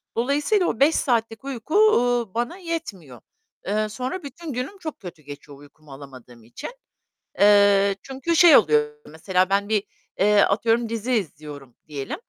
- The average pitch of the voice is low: No, high, 215 Hz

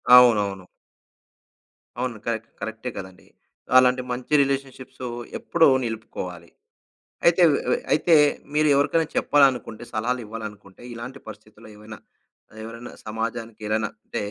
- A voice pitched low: Yes, low, 115 Hz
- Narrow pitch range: No, average, 3.1 semitones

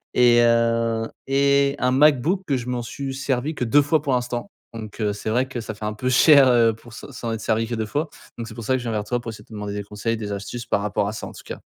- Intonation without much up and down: No, average, 3.2 semitones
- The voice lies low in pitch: Yes, low, 120 Hz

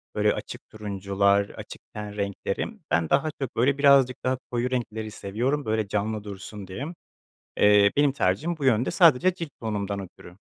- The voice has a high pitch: No, low, 110 Hz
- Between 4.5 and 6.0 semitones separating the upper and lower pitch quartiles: Yes, average, 4.8 semitones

